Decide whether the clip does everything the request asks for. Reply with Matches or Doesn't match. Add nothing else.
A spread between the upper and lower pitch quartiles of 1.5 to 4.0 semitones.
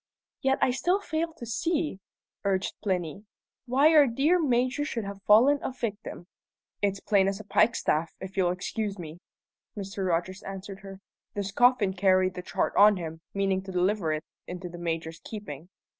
Doesn't match